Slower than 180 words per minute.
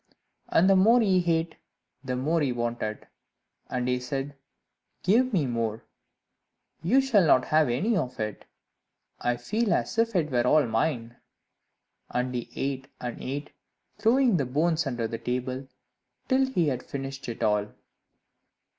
Yes: average, 150 wpm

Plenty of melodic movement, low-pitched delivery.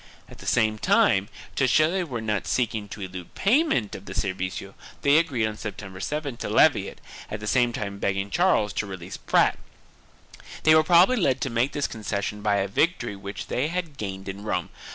Yes: wide, 6.4 semitones; low, 110 Hz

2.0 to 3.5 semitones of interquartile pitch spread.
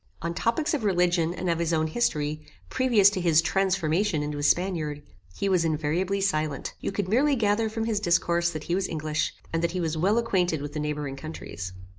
No: average, 4.3 semitones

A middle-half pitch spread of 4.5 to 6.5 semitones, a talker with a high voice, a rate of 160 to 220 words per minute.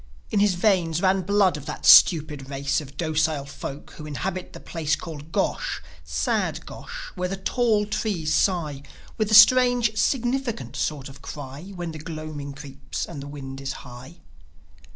No: wide, 5.5 semitones; medium, 155 Hz; average, 165 wpm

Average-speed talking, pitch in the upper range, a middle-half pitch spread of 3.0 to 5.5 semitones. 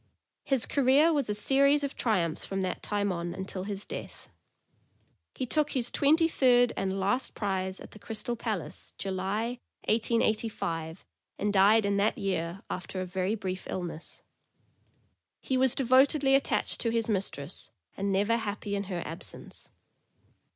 Yes: average, 150 wpm; high, 205 Hz; average, 4.6 semitones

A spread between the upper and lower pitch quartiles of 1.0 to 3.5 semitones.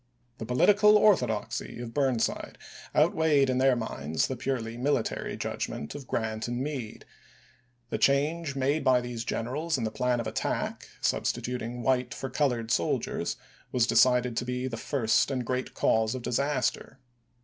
Yes: average, 3.0 semitones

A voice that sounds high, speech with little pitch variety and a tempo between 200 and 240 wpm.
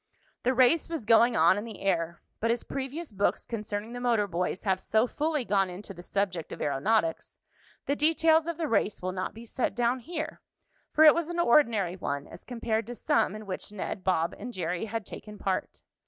No: high, 220 Hz; average, 5.1 semitones; fast, 205 wpm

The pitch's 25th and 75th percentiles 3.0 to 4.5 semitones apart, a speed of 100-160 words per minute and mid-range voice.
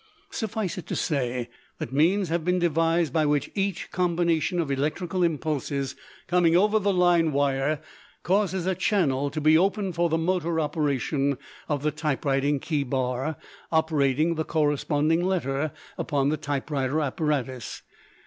Yes: average, 3.6 semitones; average, 145 wpm; medium, 155 Hz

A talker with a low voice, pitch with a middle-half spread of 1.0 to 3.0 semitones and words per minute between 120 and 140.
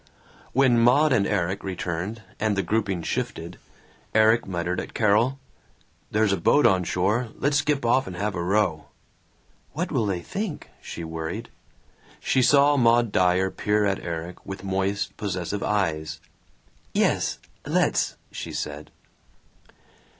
No: low, 100 Hz; average, 4.4 semitones; slow, 135 wpm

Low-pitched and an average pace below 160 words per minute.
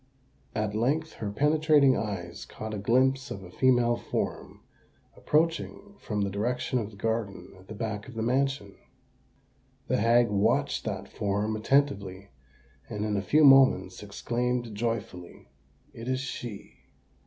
Yes: low, 115 Hz; average, 145 wpm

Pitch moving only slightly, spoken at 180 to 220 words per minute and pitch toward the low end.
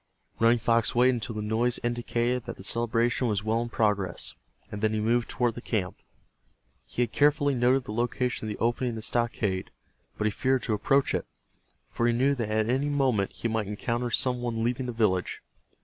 Yes: narrow, 2.2 semitones; fast, 205 wpm; low, 120 Hz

